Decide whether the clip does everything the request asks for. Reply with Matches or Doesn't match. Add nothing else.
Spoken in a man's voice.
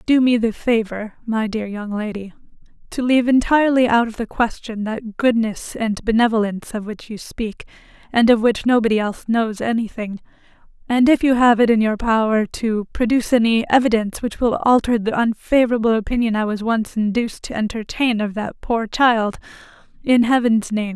Doesn't match